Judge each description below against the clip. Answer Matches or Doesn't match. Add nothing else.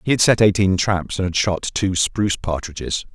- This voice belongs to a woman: Doesn't match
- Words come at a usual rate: Doesn't match